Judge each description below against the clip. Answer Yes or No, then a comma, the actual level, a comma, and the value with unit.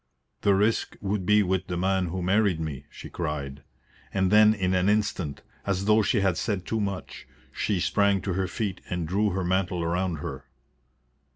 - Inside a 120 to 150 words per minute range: No, average, 185 wpm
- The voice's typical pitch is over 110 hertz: No, very low, 95 Hz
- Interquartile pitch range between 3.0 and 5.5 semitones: No, narrow, 2.5 semitones